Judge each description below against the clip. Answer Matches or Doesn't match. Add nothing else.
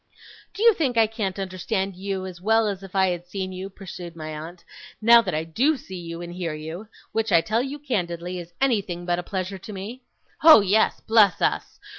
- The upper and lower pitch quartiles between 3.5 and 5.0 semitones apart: Matches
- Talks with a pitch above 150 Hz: Matches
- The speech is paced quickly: Matches